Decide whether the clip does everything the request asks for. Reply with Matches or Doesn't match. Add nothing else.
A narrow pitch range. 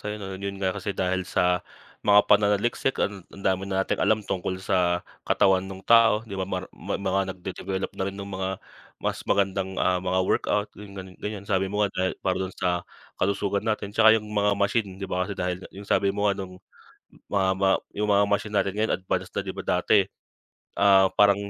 Matches